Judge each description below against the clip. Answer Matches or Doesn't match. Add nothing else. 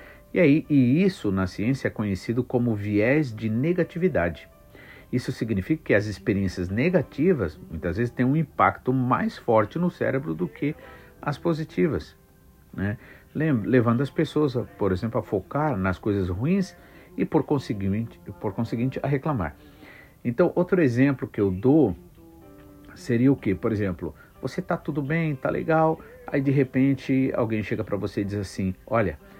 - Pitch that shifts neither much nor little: Doesn't match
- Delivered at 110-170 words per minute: Matches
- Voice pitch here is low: Matches